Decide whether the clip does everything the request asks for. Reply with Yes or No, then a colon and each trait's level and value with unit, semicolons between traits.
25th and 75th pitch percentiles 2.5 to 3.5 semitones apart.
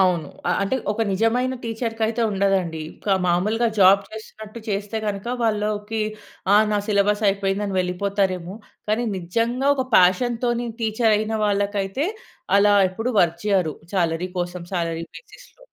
Yes: average, 3.2 semitones